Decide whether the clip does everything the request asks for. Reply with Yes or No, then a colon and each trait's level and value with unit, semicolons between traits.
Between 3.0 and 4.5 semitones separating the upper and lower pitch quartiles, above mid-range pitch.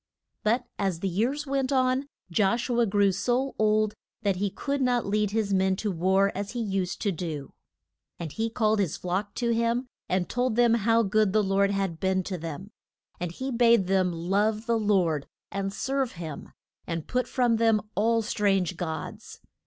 Yes: average, 3.7 semitones; high, 205 Hz